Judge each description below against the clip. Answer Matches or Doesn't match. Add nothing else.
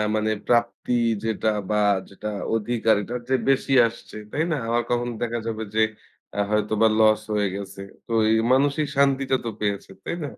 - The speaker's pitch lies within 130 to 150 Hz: Doesn't match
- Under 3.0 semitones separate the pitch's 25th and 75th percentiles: Matches